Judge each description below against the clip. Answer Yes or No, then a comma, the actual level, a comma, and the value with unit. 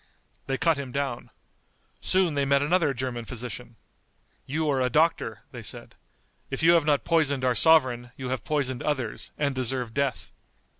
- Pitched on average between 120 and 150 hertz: Yes, low, 135 Hz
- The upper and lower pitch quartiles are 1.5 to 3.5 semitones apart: Yes, average, 3.2 semitones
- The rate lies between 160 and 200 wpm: Yes, average, 165 wpm